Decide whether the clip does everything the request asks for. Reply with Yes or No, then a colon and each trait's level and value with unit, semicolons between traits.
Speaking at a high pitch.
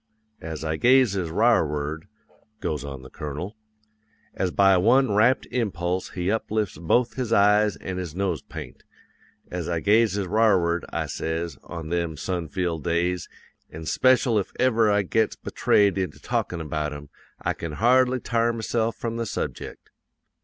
No: very low, 95 Hz